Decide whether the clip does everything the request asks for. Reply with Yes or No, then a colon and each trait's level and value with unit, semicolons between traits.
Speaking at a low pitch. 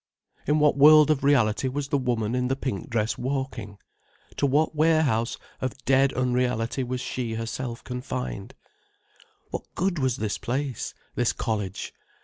Yes: low, 130 Hz